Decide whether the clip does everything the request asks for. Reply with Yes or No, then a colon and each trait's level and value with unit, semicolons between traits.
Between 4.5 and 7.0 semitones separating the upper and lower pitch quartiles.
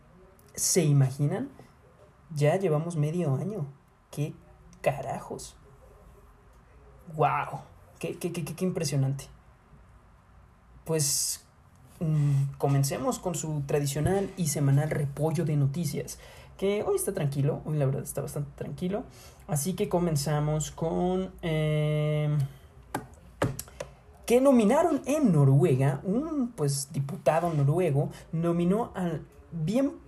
No: average, 3.9 semitones